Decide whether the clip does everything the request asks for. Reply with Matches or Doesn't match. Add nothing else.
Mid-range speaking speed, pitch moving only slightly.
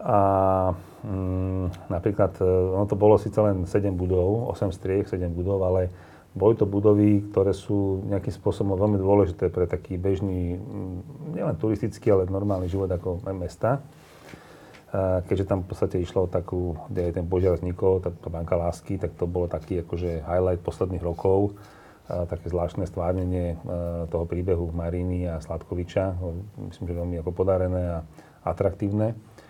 Matches